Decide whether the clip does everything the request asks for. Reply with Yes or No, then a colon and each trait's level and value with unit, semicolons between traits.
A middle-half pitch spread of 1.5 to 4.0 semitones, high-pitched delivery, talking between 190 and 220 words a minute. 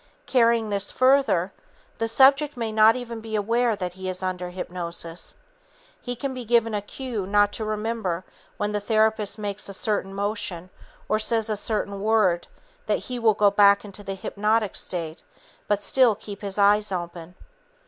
No: average, 2.7 semitones; high, 210 Hz; average, 170 wpm